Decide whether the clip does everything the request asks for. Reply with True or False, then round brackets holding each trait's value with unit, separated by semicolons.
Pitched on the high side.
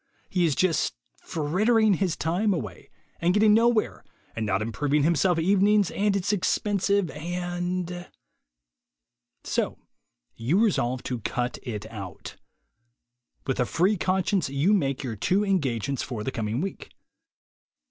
False (170 Hz)